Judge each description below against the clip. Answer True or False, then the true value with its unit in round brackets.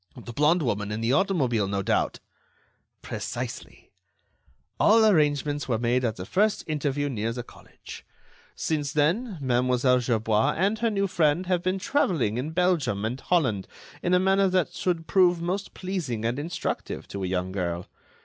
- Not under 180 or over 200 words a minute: False (160 wpm)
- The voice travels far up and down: True (7.8 semitones)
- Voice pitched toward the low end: False (145 Hz)